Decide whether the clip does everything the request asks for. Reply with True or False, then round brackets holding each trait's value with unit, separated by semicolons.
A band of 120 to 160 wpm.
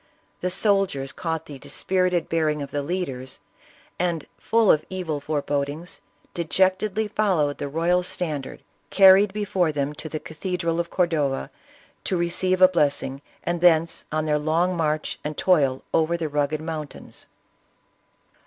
True (155 wpm)